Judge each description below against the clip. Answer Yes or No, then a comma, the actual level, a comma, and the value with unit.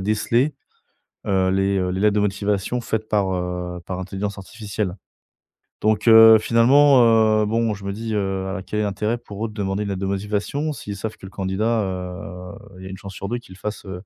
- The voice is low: Yes, low, 100 Hz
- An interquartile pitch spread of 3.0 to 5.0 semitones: No, narrow, 2.5 semitones